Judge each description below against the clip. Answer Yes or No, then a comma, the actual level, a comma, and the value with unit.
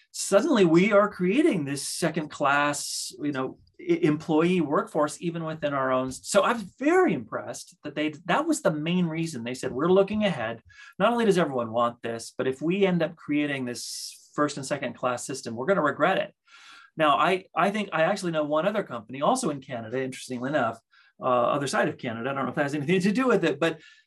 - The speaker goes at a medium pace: No, fast, 220 wpm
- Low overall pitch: No, medium, 160 Hz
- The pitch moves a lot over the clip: Yes, wide, 6.2 semitones